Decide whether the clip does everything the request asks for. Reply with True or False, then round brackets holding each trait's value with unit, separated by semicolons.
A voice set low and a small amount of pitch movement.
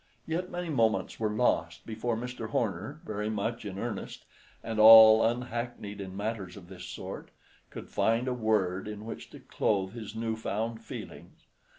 True (110 Hz; 2.3 semitones)